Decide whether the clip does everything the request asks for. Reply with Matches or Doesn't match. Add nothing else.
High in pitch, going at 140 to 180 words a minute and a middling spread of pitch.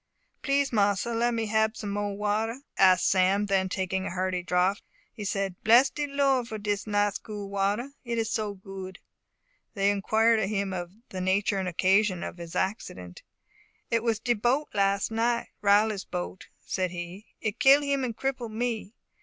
Matches